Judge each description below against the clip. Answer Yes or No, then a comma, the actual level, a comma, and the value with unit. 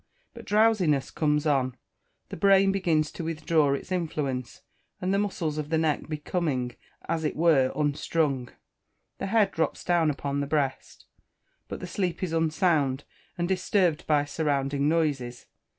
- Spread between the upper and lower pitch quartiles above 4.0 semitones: No, average, 3.6 semitones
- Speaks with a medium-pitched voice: Yes, medium, 155 Hz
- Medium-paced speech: Yes, average, 150 wpm